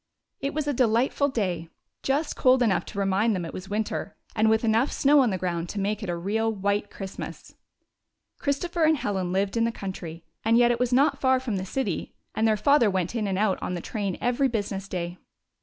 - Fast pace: Yes, fast, 225 wpm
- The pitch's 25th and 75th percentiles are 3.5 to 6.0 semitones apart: Yes, average, 4.6 semitones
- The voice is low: No, high, 215 Hz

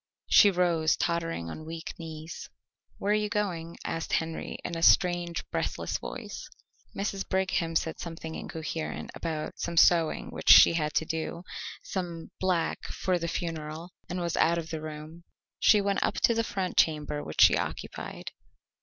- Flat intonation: Yes, narrow, 2.0 semitones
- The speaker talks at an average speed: Yes, average, 165 wpm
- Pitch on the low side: No, medium, 165 Hz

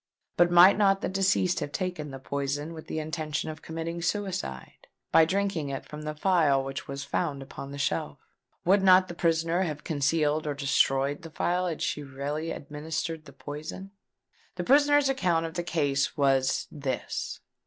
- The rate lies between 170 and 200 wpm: Yes, average, 175 wpm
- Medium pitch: Yes, medium, 155 Hz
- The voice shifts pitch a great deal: No, average, 3.7 semitones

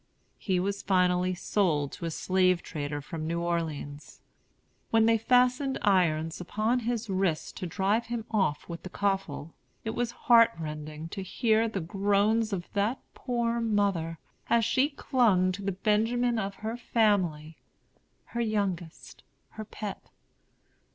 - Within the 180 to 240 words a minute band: No, average, 145 wpm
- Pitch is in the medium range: No, high, 200 Hz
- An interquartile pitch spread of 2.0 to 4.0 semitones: No, average, 4.8 semitones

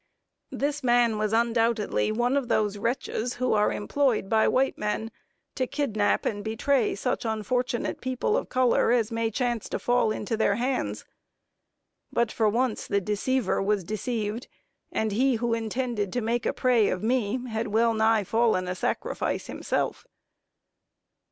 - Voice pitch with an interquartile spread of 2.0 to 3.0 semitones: Yes, average, 2.7 semitones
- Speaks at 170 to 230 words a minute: No, average, 150 wpm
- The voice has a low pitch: No, high, 230 Hz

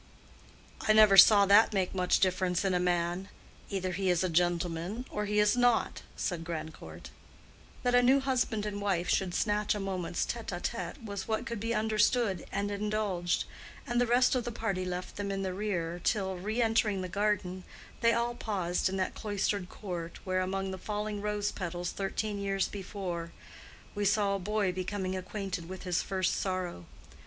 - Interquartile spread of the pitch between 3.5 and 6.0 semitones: No, narrow, 2.6 semitones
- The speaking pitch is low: No, high, 195 Hz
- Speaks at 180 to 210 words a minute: Yes, average, 185 wpm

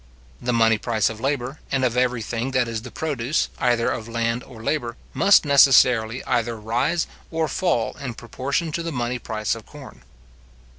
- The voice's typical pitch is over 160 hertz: No, low, 125 Hz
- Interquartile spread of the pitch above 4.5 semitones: No, average, 3.3 semitones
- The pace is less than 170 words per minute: No, average, 180 wpm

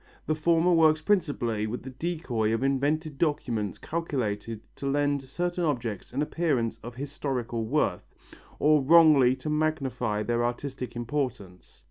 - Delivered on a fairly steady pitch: No, average, 4.6 semitones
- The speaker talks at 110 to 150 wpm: Yes, slow, 135 wpm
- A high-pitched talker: No, low, 135 Hz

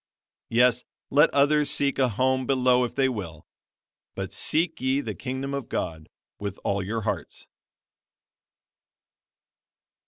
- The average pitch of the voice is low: Yes, low, 130 Hz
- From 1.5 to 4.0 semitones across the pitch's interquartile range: No, average, 5.1 semitones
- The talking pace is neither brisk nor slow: No, slow, 125 wpm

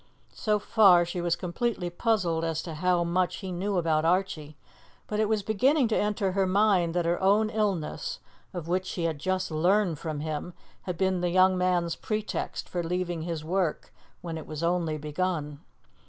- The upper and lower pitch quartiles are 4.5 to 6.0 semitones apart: No, average, 2.7 semitones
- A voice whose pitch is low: No, medium, 180 Hz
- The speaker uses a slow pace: No, average, 185 wpm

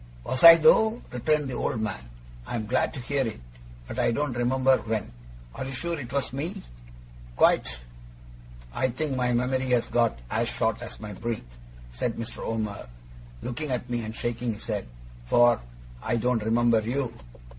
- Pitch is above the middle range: No, low, 120 Hz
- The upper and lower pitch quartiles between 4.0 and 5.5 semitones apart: No, average, 2.8 semitones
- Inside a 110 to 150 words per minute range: No, average, 170 wpm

